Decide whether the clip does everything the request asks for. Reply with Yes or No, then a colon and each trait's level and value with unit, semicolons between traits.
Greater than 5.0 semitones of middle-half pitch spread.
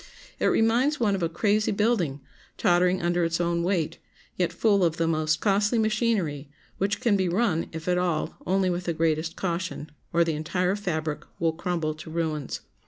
No: average, 3.6 semitones